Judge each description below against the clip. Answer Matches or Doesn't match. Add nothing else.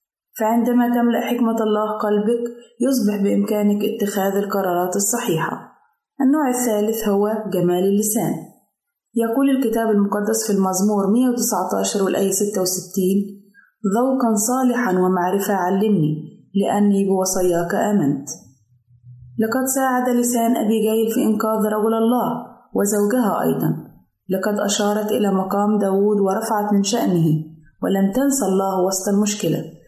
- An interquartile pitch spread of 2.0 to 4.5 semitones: Matches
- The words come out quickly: Doesn't match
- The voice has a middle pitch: Doesn't match